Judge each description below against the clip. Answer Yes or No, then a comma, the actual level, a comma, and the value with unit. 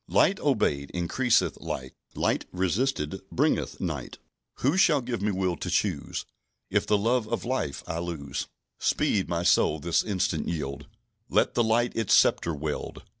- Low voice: Yes, very low, 95 Hz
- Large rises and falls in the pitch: Yes, wide, 7.1 semitones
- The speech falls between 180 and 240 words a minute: No, average, 155 wpm